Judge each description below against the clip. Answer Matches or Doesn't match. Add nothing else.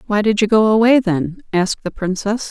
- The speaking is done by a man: Doesn't match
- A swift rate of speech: Matches